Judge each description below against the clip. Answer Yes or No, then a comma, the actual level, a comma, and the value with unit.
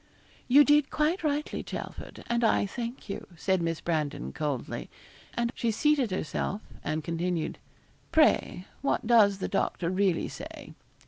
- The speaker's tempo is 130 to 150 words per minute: Yes, average, 140 wpm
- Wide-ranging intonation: Yes, wide, 7.8 semitones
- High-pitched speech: Yes, high, 200 Hz